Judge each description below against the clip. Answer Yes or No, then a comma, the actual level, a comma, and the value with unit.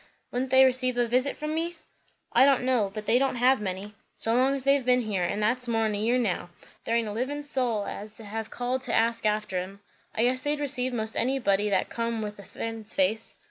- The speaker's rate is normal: No, fast, 225 wpm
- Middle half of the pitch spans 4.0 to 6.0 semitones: No, average, 3.3 semitones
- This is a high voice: Yes, high, 235 Hz